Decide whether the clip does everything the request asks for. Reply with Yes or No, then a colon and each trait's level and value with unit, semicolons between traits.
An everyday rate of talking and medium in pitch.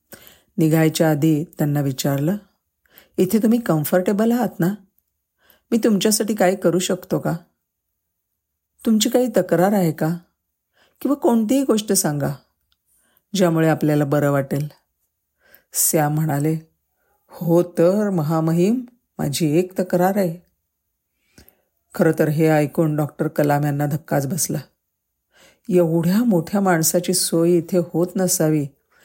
Yes: average, 110 wpm; medium, 170 Hz